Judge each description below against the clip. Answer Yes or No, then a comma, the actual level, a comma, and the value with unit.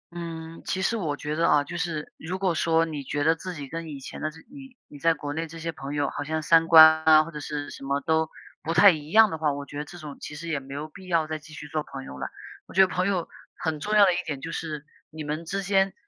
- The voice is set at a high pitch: No, medium, 160 Hz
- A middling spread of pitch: No, narrow, 2.2 semitones